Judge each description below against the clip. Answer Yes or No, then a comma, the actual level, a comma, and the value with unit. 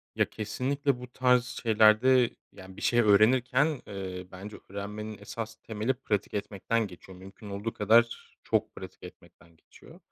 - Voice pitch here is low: Yes, low, 110 Hz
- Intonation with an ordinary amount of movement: Yes, average, 3.5 semitones